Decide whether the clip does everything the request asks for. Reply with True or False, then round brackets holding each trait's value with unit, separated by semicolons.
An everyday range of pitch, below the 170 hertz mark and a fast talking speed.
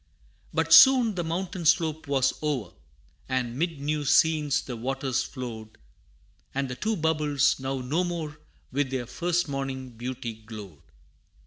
False (4.1 semitones; 140 Hz; 140 wpm)